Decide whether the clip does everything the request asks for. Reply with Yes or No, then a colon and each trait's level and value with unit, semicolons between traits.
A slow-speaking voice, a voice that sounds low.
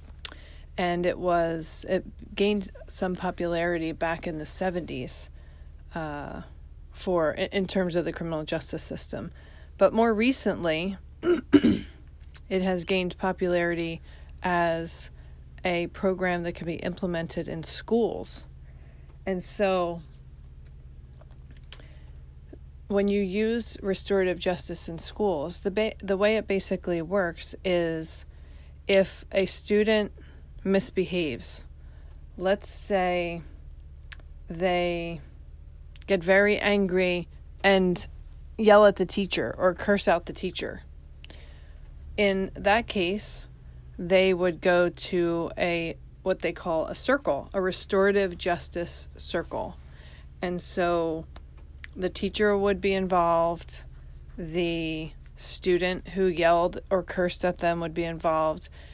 No: slow, 110 wpm; medium, 170 Hz